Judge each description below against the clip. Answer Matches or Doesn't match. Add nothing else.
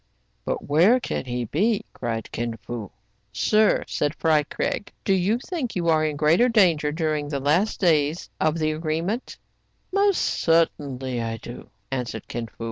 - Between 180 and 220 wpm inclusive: Matches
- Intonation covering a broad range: Matches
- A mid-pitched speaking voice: Matches